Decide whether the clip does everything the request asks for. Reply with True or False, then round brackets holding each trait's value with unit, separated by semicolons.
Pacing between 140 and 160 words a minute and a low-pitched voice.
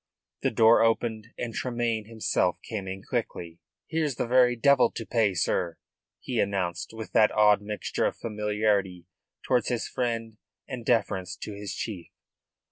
True (150 wpm; 110 Hz)